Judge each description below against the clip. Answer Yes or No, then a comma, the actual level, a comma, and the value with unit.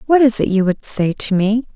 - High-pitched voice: Yes, high, 215 Hz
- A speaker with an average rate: No, fast, 275 wpm